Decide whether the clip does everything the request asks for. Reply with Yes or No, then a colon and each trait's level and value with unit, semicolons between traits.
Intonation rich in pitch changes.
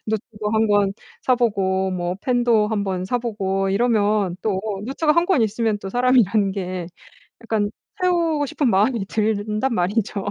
No: average, 3.7 semitones